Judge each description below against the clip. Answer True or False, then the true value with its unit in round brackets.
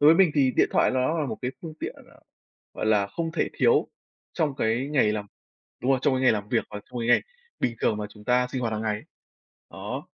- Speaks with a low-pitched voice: True (125 Hz)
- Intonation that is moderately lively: True (4.9 semitones)